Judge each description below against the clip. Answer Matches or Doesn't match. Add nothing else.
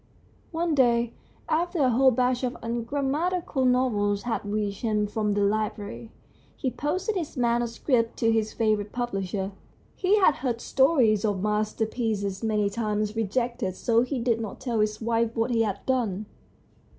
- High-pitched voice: Matches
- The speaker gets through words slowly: Doesn't match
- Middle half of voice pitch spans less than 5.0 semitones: Matches